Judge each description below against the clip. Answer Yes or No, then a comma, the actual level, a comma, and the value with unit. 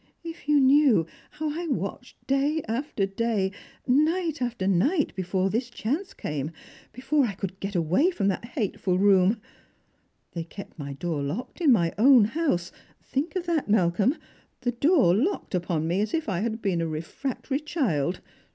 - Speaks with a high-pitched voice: Yes, high, 225 Hz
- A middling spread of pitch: No, wide, 7.8 semitones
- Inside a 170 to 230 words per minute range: Yes, average, 175 wpm